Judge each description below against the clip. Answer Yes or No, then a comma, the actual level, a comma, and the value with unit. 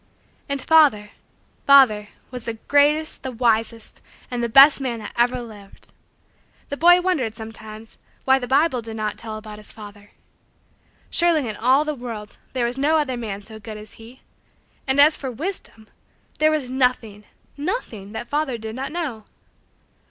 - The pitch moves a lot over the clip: No, average, 4.5 semitones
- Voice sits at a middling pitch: No, high, 245 Hz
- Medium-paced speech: Yes, average, 165 wpm